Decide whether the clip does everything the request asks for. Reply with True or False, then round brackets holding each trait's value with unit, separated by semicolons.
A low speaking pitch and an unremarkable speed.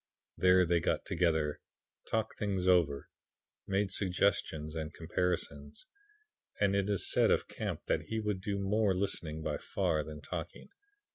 True (90 Hz; 145 wpm)